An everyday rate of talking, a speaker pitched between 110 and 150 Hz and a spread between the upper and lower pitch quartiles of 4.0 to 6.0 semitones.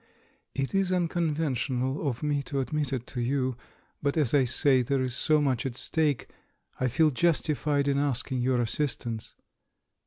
No: average, 165 wpm; medium, 140 Hz; average, 2.9 semitones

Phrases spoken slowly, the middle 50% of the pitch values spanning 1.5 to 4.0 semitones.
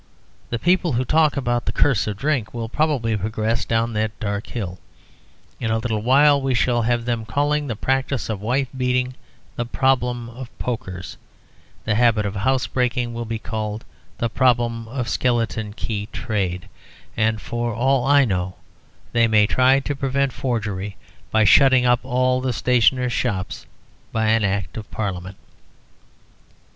No: average, 155 wpm; average, 2.9 semitones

